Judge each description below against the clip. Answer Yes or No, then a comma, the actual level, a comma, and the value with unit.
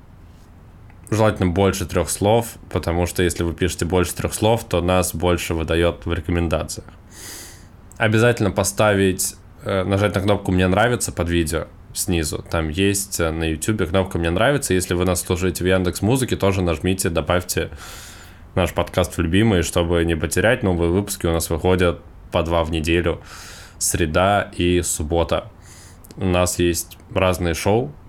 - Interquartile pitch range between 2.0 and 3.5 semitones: Yes, narrow, 2.4 semitones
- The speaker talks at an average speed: Yes, average, 145 wpm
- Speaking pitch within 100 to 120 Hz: No, very low, 90 Hz